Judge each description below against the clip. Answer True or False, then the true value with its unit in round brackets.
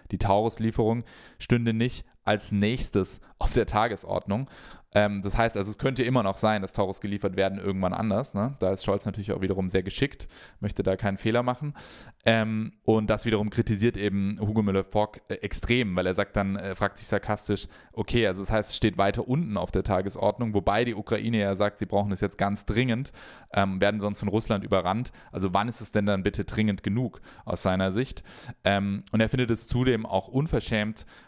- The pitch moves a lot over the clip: False (2.4 semitones)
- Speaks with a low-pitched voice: True (105 Hz)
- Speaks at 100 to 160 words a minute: False (200 wpm)